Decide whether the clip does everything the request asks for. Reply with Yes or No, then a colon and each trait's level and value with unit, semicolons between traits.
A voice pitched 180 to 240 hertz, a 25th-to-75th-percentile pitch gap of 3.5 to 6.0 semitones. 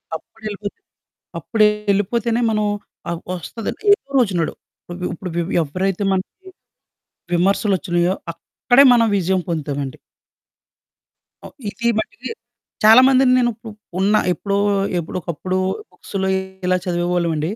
Yes: high, 190 Hz; average, 4.0 semitones